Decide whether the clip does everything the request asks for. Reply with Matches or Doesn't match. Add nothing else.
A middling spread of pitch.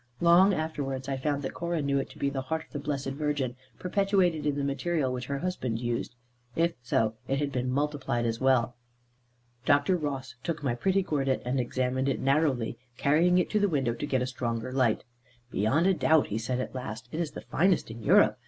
Matches